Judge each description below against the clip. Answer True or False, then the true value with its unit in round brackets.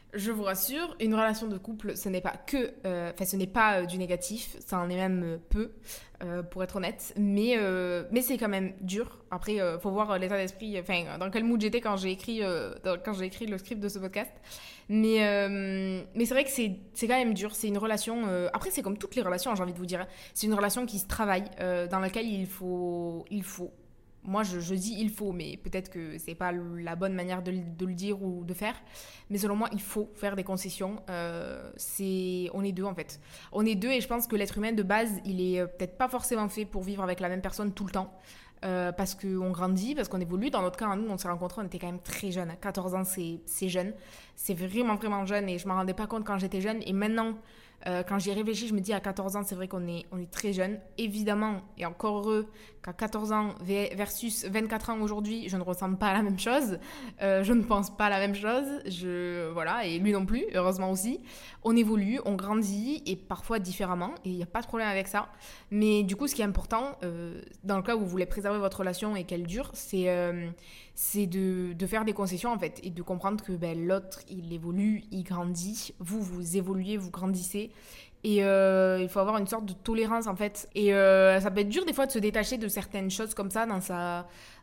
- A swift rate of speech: True (245 wpm)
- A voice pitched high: True (195 Hz)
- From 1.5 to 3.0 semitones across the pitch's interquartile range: True (2.7 semitones)